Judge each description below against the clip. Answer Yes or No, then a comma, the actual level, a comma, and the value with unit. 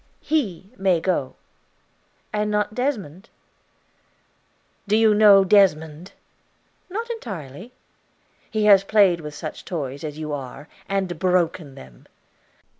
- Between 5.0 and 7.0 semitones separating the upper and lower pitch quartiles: Yes, wide, 5.4 semitones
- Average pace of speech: No, slow, 115 wpm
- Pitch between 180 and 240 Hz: Yes, high, 190 Hz